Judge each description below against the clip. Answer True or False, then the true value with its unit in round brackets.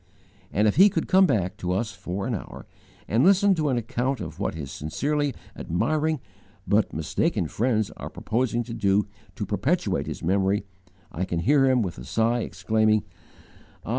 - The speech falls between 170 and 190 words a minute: True (180 wpm)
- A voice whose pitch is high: False (110 Hz)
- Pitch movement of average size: False (5.9 semitones)